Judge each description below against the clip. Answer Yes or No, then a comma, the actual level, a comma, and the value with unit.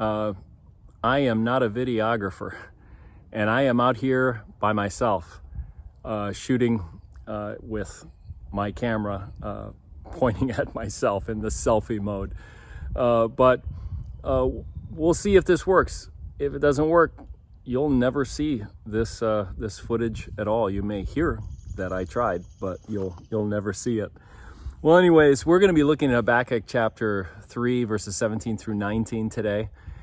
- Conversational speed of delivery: Yes, average, 150 wpm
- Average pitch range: Yes, average, 4.0 semitones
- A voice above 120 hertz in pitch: No, low, 110 Hz